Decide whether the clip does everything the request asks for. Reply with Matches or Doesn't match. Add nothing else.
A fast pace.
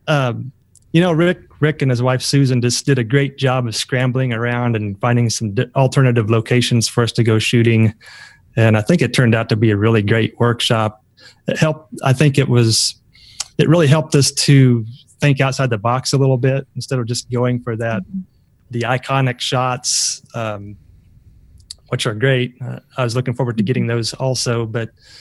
Doesn't match